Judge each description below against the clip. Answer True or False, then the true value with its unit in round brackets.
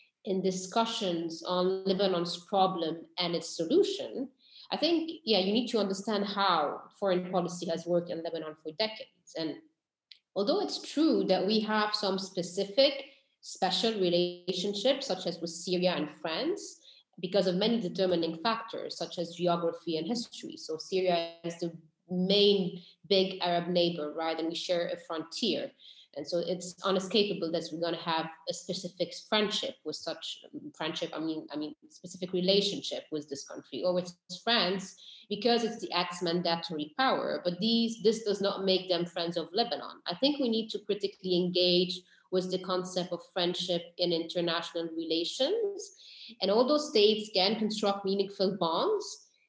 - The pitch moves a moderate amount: True (4.0 semitones)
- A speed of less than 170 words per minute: True (160 wpm)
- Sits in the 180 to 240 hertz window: True (185 Hz)